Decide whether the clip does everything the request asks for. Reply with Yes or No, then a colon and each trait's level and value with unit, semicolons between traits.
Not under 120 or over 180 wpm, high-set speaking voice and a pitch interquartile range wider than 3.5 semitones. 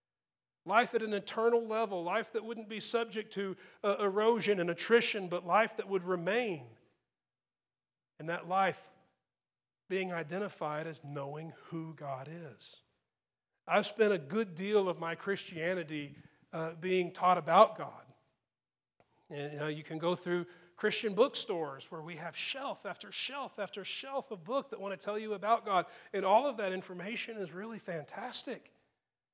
Yes: average, 155 wpm; high, 195 Hz; average, 4.2 semitones